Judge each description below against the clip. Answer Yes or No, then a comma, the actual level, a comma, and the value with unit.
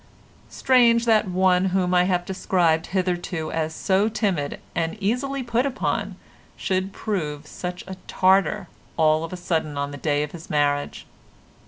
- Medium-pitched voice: Yes, medium, 180 Hz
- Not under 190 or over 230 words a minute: No, average, 155 wpm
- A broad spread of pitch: No, average, 3.9 semitones